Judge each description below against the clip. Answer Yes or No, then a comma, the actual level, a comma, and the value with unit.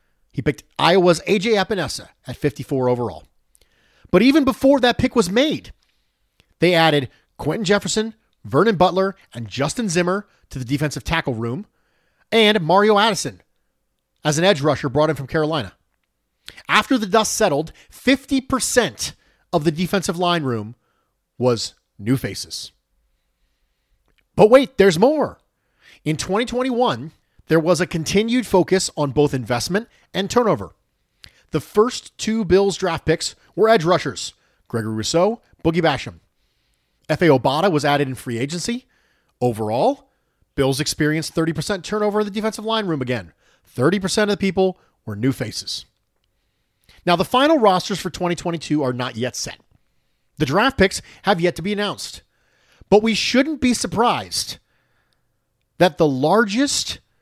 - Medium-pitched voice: Yes, medium, 175 Hz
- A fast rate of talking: No, average, 140 wpm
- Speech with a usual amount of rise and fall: No, wide, 7.7 semitones